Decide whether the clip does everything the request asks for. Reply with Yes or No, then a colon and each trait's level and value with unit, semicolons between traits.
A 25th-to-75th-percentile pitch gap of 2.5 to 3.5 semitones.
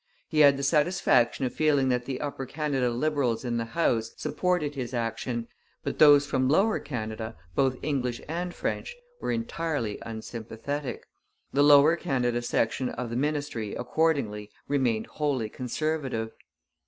No: average, 4.2 semitones